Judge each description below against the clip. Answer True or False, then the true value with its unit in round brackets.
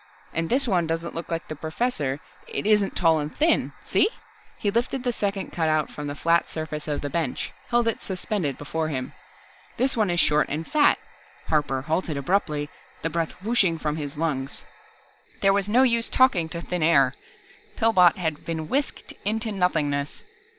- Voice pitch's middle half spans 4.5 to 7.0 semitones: True (5.4 semitones)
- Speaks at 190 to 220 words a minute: False (180 wpm)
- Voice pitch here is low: False (165 Hz)